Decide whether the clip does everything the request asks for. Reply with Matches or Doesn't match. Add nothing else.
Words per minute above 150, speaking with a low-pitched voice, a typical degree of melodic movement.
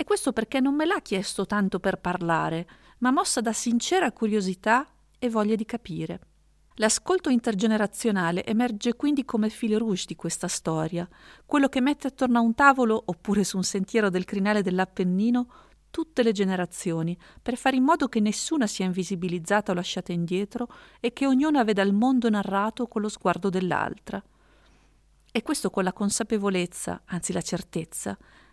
Doesn't match